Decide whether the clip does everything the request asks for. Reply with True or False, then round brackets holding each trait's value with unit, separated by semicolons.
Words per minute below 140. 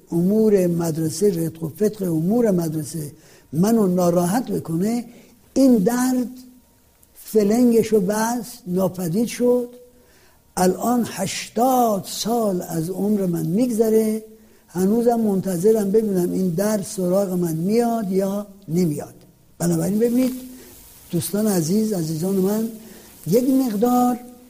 True (105 wpm)